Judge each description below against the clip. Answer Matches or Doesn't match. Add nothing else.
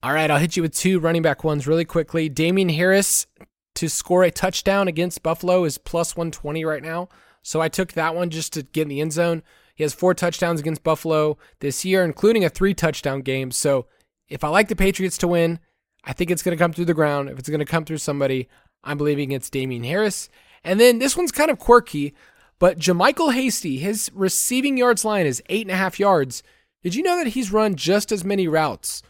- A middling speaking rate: Doesn't match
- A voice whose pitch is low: Doesn't match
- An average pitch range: Matches